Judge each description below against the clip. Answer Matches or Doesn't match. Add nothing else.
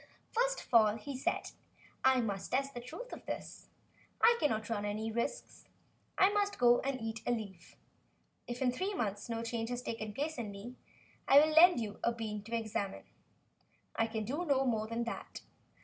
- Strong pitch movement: Doesn't match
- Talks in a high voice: Matches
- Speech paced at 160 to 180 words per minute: Doesn't match